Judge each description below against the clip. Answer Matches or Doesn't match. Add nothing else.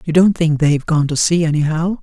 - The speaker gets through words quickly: Matches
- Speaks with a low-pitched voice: Doesn't match